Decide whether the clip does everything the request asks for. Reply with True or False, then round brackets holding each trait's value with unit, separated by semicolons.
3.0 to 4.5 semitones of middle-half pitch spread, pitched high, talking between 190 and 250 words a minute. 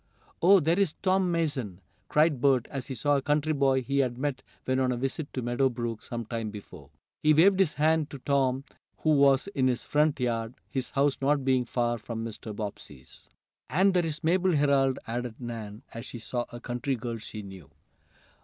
False (3.9 semitones; 130 Hz; 195 wpm)